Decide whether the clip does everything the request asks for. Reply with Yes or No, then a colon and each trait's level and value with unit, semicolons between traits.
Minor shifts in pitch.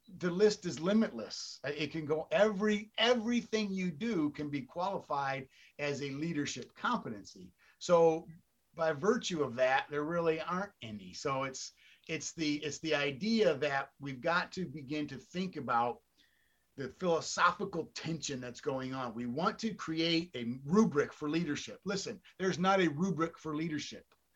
No: average, 4.6 semitones